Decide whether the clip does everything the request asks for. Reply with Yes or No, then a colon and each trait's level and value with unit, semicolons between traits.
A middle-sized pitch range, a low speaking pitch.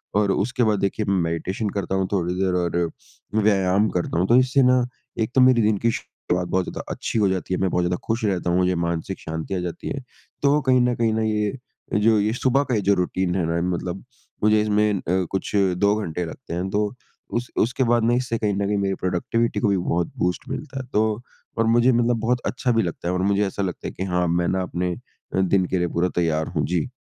Yes: average, 4.0 semitones; low, 100 Hz